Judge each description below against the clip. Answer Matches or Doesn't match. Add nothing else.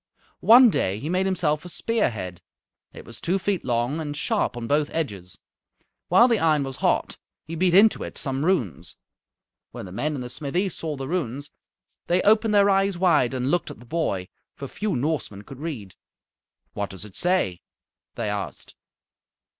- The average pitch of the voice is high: Doesn't match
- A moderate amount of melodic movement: Doesn't match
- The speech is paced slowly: Doesn't match